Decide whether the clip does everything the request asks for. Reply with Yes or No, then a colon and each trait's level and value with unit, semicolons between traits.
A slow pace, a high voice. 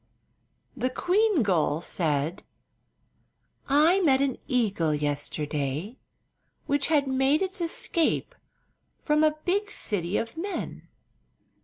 Yes: slow, 105 wpm; very high, 265 Hz